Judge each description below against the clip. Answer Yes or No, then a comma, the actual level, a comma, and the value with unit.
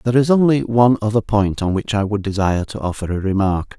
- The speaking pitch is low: Yes, low, 105 Hz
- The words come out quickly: Yes, fast, 240 wpm